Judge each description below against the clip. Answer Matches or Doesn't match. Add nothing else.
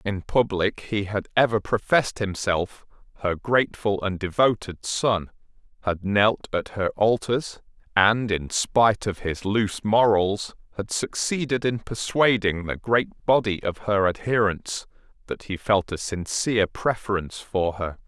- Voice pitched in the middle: Doesn't match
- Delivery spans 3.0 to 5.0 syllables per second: Matches